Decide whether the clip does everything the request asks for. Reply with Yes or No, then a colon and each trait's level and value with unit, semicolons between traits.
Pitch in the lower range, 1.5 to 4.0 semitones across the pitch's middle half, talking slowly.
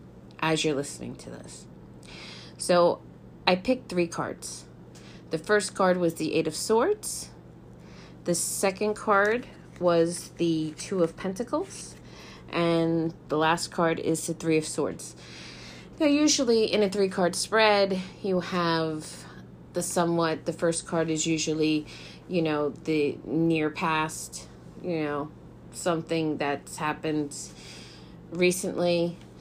No: medium, 165 Hz; average, 3.7 semitones; slow, 125 wpm